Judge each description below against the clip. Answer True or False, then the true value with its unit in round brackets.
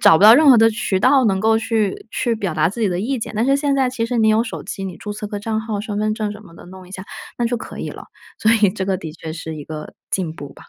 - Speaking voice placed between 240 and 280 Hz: False (215 Hz)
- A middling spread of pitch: True (3.3 semitones)